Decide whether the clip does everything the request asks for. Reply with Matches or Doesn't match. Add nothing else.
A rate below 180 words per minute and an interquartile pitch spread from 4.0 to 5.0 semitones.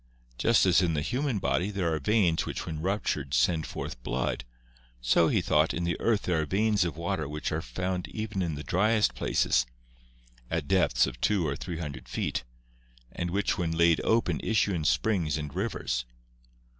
Doesn't match